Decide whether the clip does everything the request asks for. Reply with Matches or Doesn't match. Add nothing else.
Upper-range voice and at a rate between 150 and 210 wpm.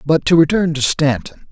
Doesn't match